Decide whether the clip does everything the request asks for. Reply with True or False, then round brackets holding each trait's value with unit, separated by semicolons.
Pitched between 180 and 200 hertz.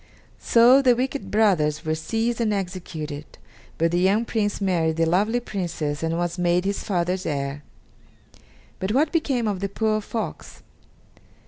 True (190 Hz)